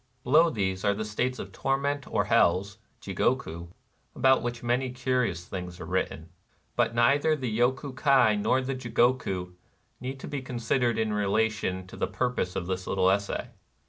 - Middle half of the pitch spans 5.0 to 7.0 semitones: Yes, average, 5.3 semitones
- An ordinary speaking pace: Yes, average, 165 wpm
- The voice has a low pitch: Yes, low, 115 Hz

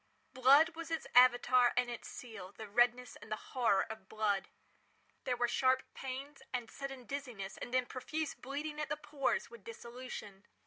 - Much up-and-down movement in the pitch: No, average, 2.9 semitones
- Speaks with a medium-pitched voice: No, very high, 250 Hz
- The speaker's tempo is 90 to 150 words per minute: No, average, 165 wpm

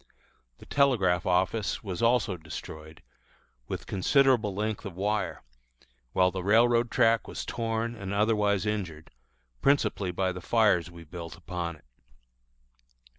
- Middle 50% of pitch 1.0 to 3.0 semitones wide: No, average, 4.2 semitones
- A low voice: Yes, low, 100 Hz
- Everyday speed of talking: No, slow, 125 wpm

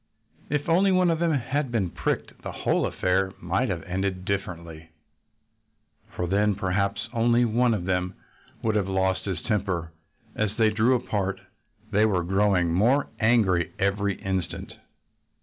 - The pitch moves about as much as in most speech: Yes, average, 3.9 semitones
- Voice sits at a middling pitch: No, low, 100 Hz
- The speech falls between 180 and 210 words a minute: No, average, 150 wpm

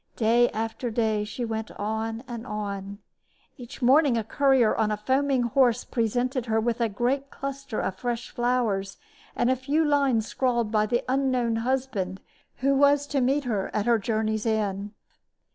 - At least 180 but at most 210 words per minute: No, average, 165 wpm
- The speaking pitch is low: No, high, 235 Hz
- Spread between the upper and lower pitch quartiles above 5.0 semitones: No, average, 3.2 semitones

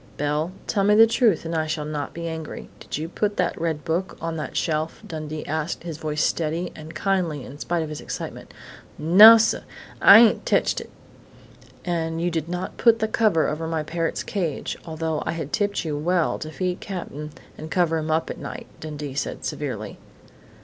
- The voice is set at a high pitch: No, medium, 165 Hz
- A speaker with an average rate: Yes, average, 190 wpm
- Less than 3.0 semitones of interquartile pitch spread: Yes, narrow, 2.5 semitones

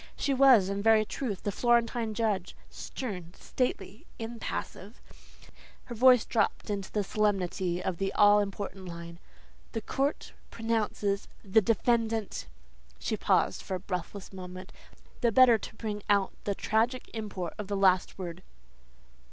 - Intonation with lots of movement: No, average, 3.2 semitones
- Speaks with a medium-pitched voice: No, high, 205 Hz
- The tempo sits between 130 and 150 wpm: Yes, average, 145 wpm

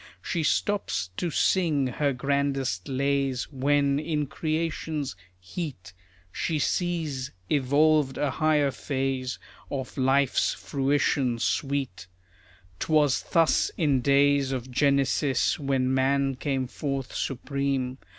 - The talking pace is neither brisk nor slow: No, slow, 105 wpm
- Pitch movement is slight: Yes, narrow, 2.1 semitones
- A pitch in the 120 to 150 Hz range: Yes, medium, 140 Hz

